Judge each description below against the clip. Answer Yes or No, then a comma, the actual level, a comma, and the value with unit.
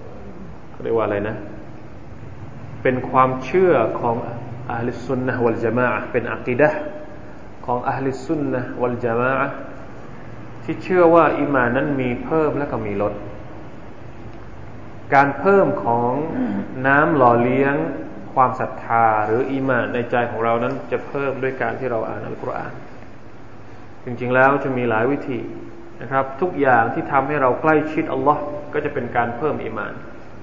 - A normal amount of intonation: Yes, average, 3.1 semitones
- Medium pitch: No, low, 125 Hz